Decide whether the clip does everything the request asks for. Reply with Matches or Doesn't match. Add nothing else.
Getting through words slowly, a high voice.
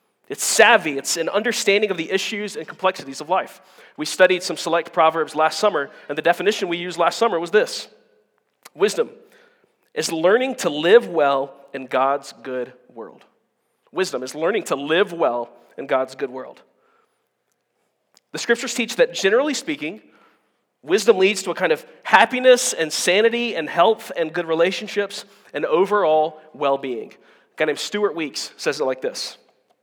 Doesn't match